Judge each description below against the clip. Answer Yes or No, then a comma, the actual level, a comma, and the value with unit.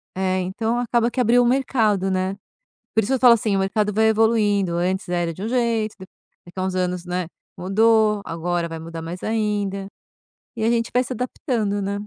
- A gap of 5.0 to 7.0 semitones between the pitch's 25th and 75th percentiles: No, average, 3.6 semitones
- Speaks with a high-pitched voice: Yes, high, 205 Hz